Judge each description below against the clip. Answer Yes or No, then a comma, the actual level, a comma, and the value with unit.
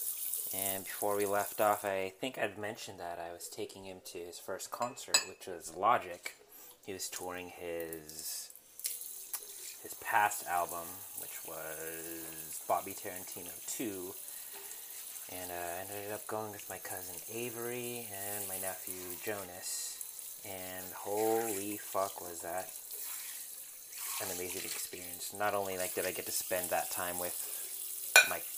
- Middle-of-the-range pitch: No, very low, 95 Hz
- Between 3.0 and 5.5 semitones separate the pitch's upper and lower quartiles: No, narrow, 2.6 semitones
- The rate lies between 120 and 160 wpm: Yes, average, 140 wpm